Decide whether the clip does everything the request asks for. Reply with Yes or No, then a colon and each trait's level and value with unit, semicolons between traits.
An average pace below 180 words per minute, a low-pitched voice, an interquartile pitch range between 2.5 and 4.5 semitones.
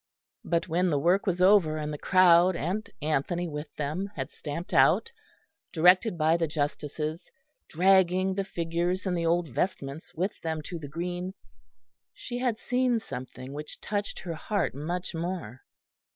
No: average, 155 wpm; medium, 170 Hz; average, 3.3 semitones